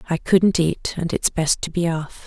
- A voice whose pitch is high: No, medium, 170 Hz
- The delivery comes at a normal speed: No, fast, 240 wpm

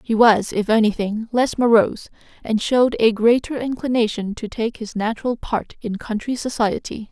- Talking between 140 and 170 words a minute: Yes, average, 160 wpm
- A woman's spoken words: Yes, female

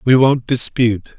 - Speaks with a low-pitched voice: Yes, low, 120 Hz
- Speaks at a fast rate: No, average, 150 wpm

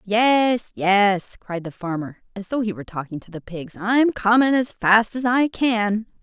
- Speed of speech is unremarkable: Yes, average, 195 wpm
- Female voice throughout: Yes, female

